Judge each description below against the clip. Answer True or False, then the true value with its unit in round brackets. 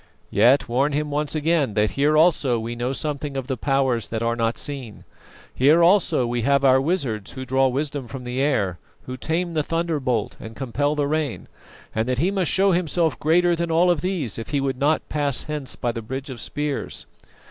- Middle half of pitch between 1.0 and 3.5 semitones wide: False (3.9 semitones)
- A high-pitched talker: False (140 Hz)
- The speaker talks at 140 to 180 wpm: False (205 wpm)